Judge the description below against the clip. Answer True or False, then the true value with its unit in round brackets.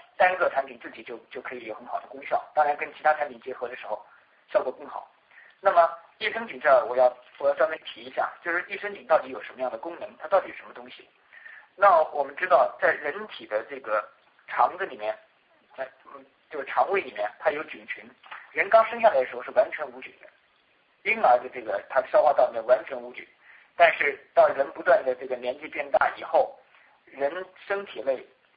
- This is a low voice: False (170 Hz)